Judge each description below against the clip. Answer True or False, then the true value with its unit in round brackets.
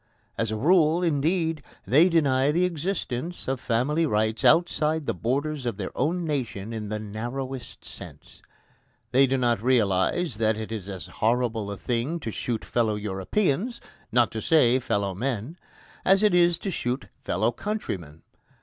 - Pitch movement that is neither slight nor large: False (6.6 semitones)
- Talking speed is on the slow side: False (160 wpm)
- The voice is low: True (125 Hz)